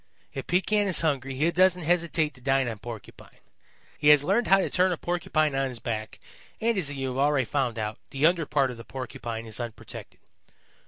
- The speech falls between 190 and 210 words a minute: Yes, fast, 205 wpm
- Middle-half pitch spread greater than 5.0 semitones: Yes, wide, 5.5 semitones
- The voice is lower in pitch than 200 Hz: Yes, medium, 140 Hz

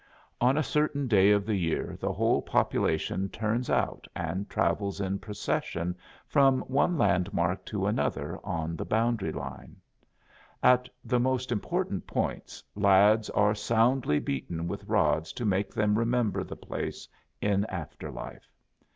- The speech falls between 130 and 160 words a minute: Yes, average, 140 wpm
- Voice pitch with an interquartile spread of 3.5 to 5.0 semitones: Yes, average, 4.3 semitones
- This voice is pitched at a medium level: No, low, 105 Hz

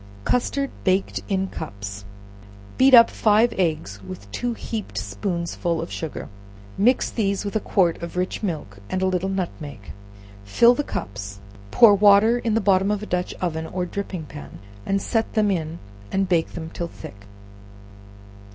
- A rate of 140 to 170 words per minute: Yes, average, 160 wpm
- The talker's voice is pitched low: No, medium, 185 Hz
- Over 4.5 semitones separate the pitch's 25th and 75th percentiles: Yes, average, 4.9 semitones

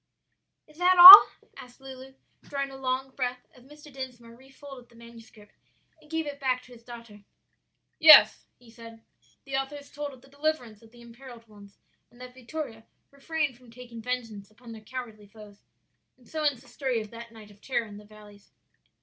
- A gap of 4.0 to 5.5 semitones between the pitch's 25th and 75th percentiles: No, average, 3.0 semitones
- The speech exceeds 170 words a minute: Yes, average, 190 wpm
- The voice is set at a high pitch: Yes, very high, 250 Hz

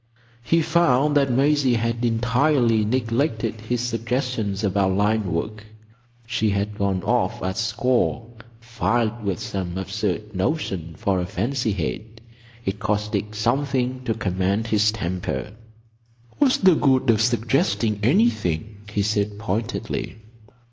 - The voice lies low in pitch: Yes, low, 110 Hz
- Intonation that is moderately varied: Yes, average, 3.3 semitones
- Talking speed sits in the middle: No, slow, 125 wpm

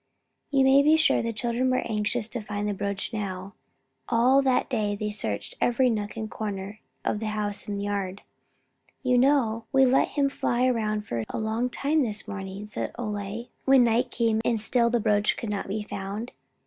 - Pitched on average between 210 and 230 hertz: Yes, high, 220 Hz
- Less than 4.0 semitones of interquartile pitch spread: Yes, average, 3.2 semitones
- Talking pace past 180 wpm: Yes, average, 195 wpm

